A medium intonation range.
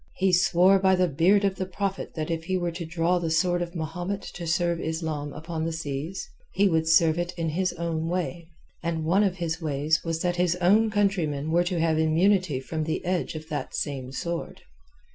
No: narrow, 2.2 semitones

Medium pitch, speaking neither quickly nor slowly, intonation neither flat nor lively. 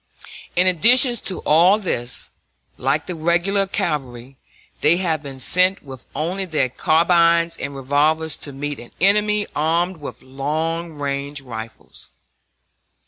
No: medium, 160 Hz; slow, 130 wpm; average, 4.4 semitones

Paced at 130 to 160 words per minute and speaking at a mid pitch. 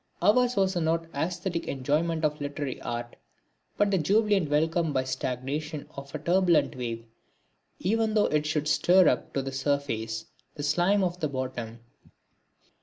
Yes: average, 155 wpm; medium, 155 Hz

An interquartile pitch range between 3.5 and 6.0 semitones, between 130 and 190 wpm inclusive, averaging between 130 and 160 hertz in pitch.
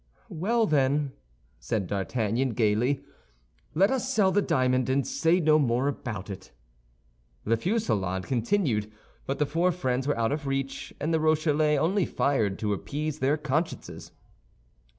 Yes: average, 5.3 semitones; average, 145 wpm; medium, 140 Hz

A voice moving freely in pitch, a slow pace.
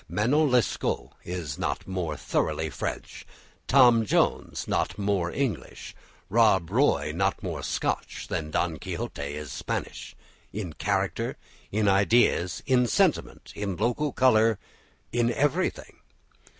Yes: wide, 5.9 semitones; slow, 120 wpm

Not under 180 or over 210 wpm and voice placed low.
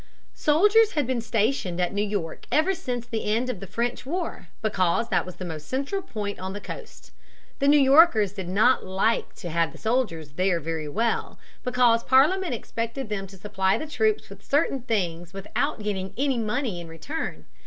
No: average, 185 wpm; high, 220 Hz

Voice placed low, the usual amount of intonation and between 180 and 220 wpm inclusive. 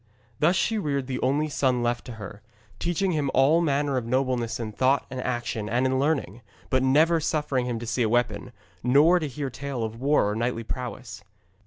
Yes: low, 130 Hz; average, 3.4 semitones; fast, 205 wpm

